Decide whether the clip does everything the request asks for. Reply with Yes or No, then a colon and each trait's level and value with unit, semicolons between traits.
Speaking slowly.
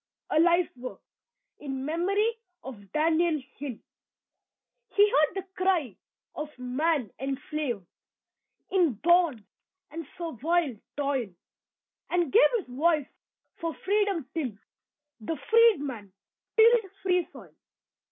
Yes: slow, 105 wpm